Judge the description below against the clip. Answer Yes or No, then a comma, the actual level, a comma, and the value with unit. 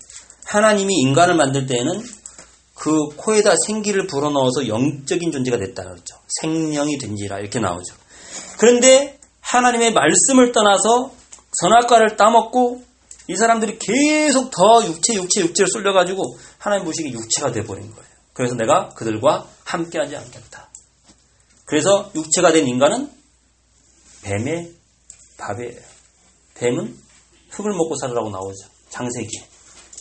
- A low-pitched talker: No, medium, 165 Hz